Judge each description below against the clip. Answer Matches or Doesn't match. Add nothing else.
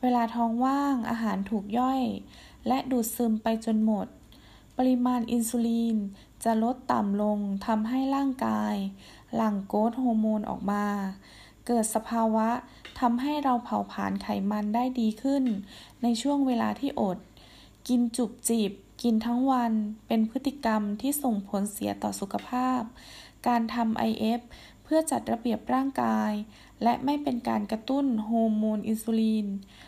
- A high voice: Matches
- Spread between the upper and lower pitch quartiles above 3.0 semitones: Doesn't match